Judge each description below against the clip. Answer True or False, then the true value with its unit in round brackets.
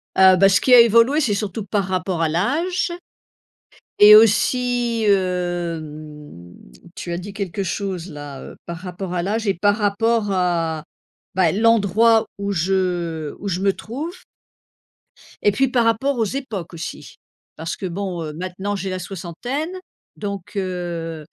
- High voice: True (195 Hz)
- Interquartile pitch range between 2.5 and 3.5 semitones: False (4.2 semitones)